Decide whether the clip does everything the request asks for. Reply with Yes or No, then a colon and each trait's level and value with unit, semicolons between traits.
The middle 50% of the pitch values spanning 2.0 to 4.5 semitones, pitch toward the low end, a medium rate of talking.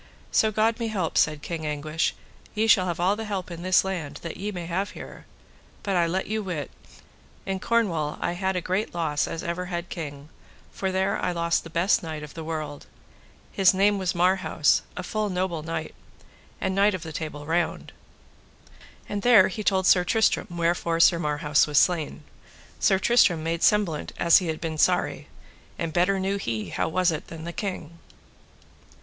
No: average, 3.0 semitones; medium, 175 Hz; average, 190 wpm